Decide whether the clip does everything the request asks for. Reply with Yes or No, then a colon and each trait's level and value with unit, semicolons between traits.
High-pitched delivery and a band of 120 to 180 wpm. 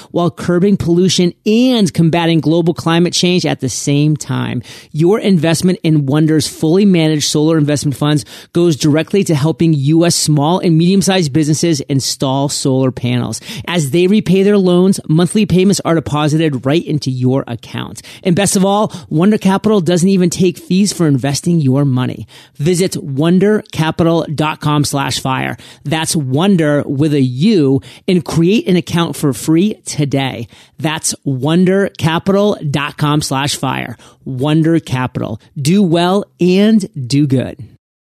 No: medium, 160 Hz; average, 140 wpm